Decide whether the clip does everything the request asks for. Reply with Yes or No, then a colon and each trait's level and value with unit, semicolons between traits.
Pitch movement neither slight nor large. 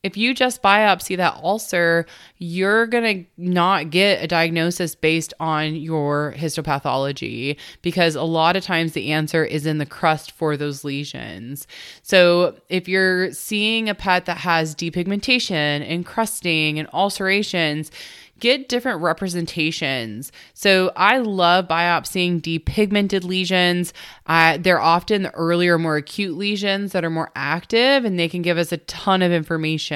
Yes: average, 3.2 semitones